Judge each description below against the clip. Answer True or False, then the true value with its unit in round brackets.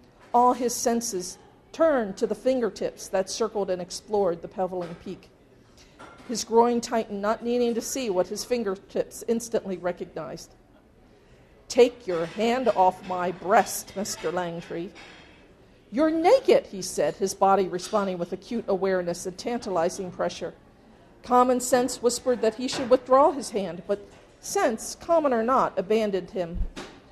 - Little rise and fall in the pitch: False (4.6 semitones)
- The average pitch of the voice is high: True (215 Hz)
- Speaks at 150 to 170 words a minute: False (140 wpm)